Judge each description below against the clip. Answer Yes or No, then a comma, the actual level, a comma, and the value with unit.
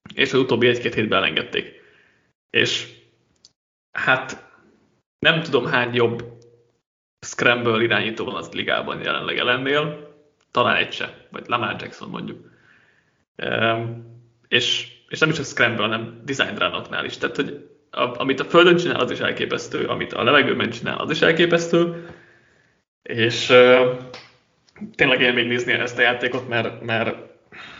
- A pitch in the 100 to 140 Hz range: Yes, low, 120 Hz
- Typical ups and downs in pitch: Yes, average, 3.1 semitones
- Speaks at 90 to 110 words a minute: No, average, 140 wpm